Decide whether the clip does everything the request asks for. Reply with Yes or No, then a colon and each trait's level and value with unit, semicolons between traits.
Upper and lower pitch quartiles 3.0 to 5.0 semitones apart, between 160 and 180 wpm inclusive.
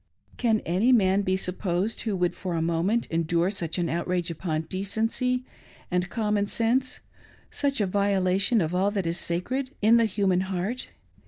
Yes: average, 3.9 semitones; average, 170 wpm